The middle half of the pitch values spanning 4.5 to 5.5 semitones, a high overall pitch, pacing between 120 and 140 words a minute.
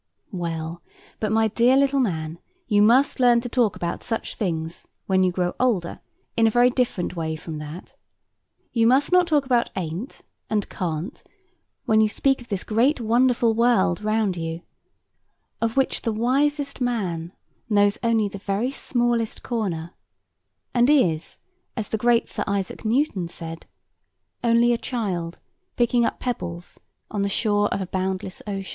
No: average, 5.1 semitones; high, 215 Hz; average, 160 wpm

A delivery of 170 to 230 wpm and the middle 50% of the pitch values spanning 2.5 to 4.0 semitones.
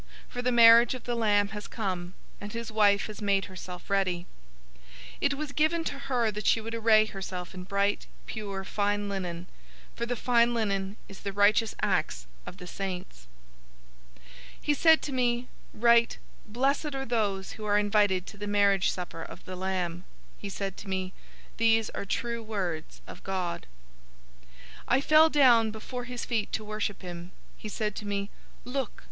Yes: average, 175 wpm; average, 3.4 semitones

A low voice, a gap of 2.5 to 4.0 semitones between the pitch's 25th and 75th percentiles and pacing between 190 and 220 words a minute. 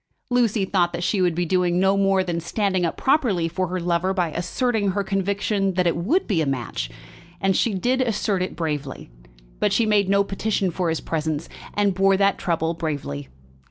No: medium, 185 Hz; average, 2.9 semitones; average, 195 wpm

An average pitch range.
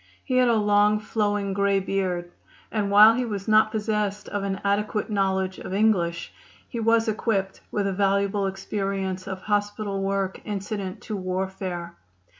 No: narrow, 1.7 semitones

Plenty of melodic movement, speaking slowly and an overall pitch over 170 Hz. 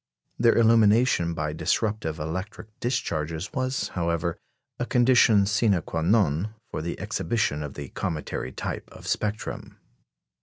No: wide, 6.1 semitones; slow, 125 wpm; low, 100 Hz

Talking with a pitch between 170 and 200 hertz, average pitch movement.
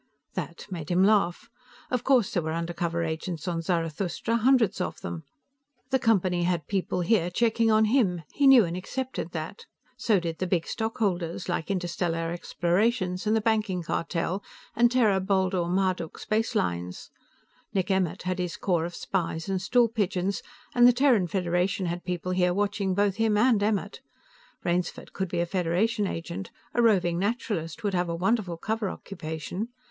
Yes: medium, 185 Hz; average, 3.9 semitones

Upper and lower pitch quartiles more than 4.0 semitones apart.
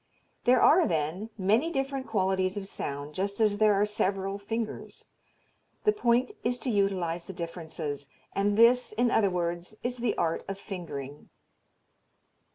Yes: average, 4.9 semitones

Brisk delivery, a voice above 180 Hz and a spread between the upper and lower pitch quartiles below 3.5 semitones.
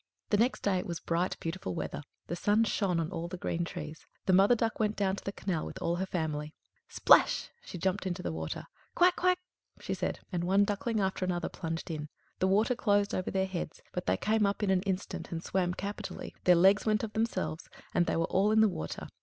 Yes: fast, 230 wpm; high, 190 Hz; average, 3.1 semitones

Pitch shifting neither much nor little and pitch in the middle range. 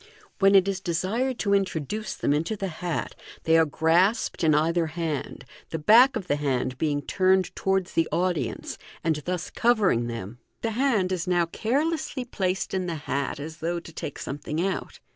Yes: average, 3.9 semitones; medium, 175 Hz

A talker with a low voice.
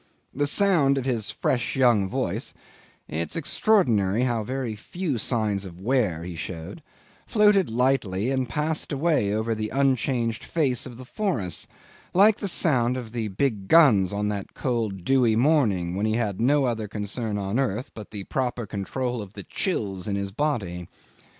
Yes: low, 115 Hz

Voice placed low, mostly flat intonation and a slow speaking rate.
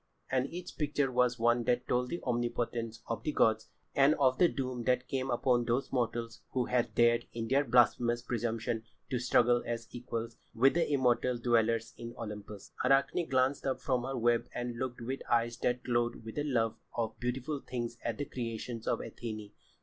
No: low, 120 Hz; narrow, 1.8 semitones; average, 190 wpm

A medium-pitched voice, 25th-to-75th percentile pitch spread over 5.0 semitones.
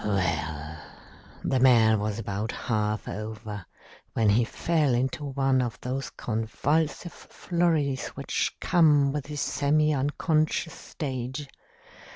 No: low, 130 Hz; wide, 5.5 semitones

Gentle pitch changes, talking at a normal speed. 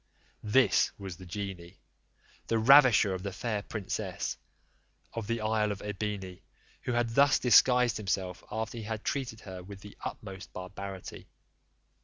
No: average, 3.1 semitones; average, 145 wpm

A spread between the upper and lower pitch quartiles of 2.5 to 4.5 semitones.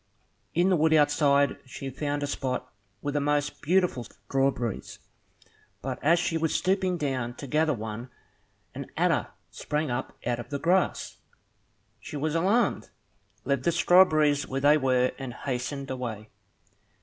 Yes: average, 3.5 semitones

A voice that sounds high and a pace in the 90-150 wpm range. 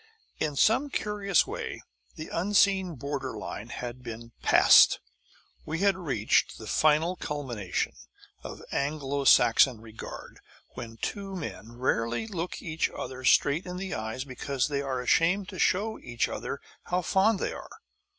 No: medium, 145 Hz; average, 145 wpm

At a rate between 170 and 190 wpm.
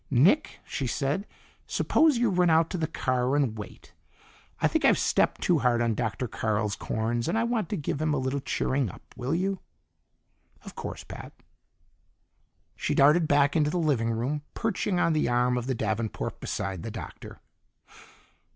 Yes: average, 175 wpm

